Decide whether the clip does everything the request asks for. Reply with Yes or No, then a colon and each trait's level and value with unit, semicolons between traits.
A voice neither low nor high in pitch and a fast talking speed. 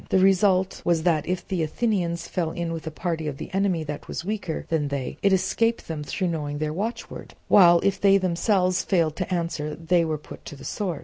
Yes: medium, 170 Hz; fast, 215 wpm